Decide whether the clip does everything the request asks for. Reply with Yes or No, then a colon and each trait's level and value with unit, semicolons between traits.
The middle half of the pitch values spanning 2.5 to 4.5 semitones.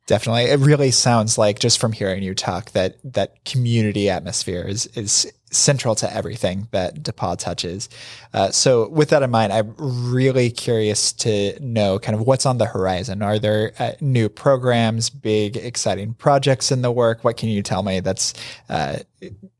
Yes: average, 3.6 semitones